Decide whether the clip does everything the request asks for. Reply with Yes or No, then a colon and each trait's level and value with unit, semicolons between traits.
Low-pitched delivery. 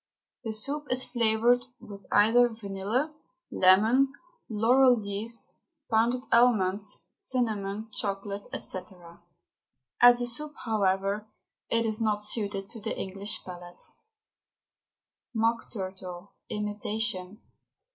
No: high, 215 Hz